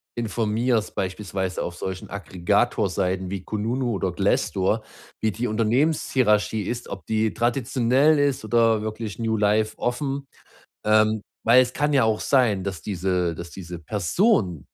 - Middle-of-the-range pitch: No, low, 110 Hz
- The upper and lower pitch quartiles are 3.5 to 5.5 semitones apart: Yes, average, 4.0 semitones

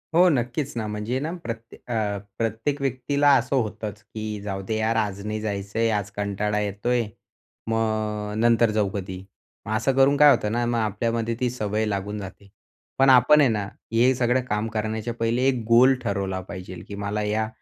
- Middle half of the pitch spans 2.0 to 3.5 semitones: Yes, narrow, 2.5 semitones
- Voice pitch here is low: Yes, low, 110 Hz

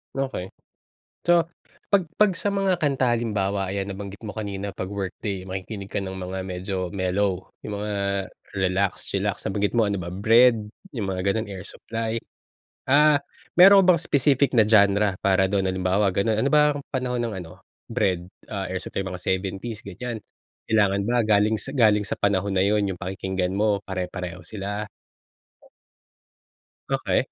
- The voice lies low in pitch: Yes, low, 100 Hz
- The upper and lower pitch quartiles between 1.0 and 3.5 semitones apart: Yes, average, 3.2 semitones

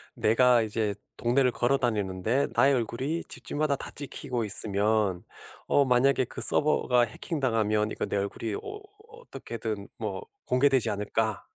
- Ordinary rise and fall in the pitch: Yes, average, 4.3 semitones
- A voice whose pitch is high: No, low, 120 Hz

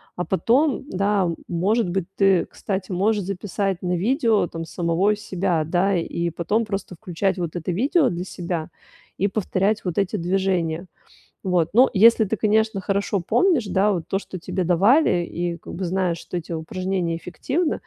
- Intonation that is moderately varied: Yes, average, 3.1 semitones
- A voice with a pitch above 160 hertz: Yes, high, 190 Hz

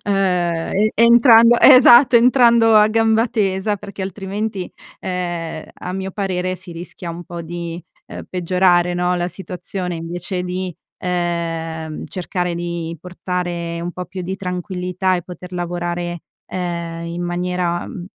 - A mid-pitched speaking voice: Yes, medium, 180 Hz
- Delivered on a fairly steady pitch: Yes, narrow, 1.9 semitones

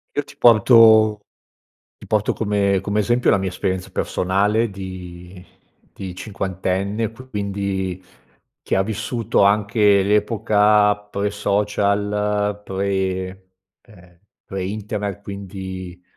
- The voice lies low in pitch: Yes, low, 100 Hz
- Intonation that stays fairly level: Yes, narrow, 1.7 semitones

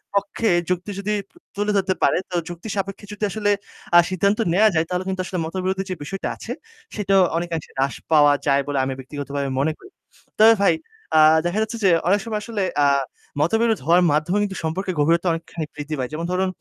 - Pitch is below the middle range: No, medium, 185 Hz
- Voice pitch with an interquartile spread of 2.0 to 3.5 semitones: No, average, 4.2 semitones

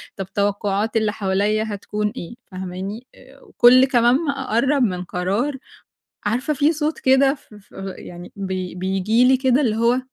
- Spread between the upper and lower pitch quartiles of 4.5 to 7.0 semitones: Yes, average, 4.8 semitones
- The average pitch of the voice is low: No, high, 220 Hz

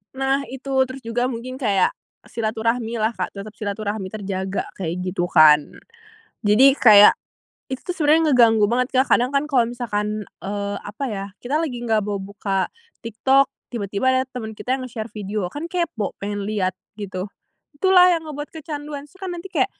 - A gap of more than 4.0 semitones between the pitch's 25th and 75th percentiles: Yes, average, 4.9 semitones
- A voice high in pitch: Yes, high, 230 Hz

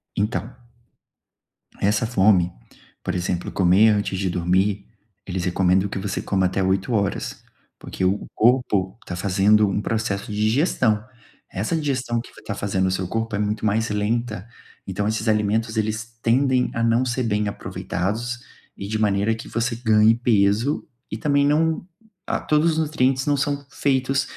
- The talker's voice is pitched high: No, low, 110 Hz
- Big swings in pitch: No, average, 3.5 semitones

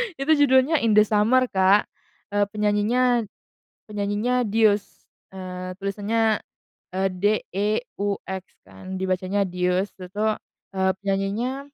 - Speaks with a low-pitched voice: No, high, 205 Hz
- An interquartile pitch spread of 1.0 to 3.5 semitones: Yes, average, 2.8 semitones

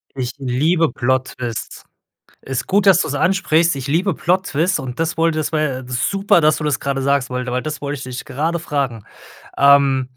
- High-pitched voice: No, medium, 145 Hz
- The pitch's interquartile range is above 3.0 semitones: Yes, average, 3.9 semitones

